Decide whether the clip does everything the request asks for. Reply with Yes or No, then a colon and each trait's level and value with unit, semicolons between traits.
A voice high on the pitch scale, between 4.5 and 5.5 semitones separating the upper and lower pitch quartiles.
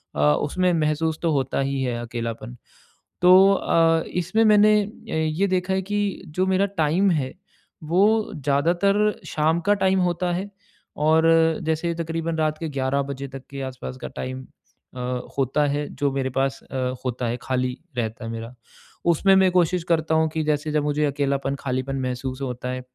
No: medium, 155 Hz; average, 5.1 semitones